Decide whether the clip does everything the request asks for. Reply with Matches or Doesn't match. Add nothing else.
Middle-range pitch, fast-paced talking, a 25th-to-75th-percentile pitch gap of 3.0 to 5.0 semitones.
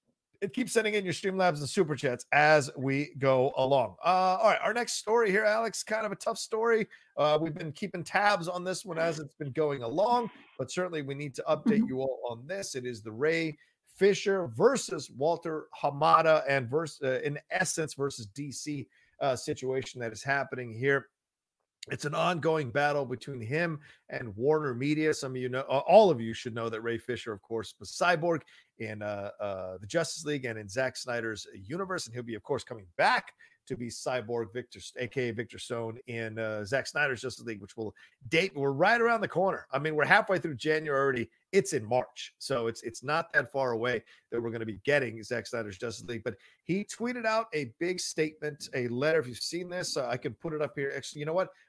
Doesn't match